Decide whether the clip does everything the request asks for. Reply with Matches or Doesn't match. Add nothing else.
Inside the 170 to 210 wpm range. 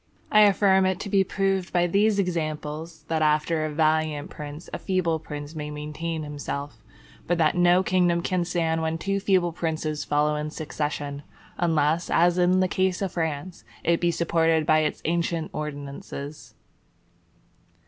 Doesn't match